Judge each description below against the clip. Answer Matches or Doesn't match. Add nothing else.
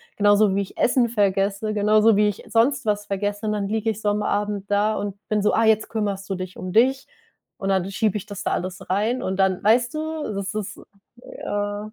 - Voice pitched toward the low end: Doesn't match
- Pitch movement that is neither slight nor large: Doesn't match